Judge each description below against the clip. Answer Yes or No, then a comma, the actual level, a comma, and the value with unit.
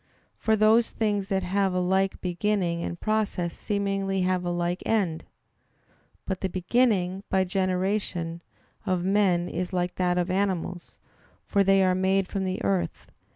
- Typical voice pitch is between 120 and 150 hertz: No, medium, 185 Hz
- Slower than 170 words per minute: Yes, average, 155 wpm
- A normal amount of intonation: No, narrow, 1.9 semitones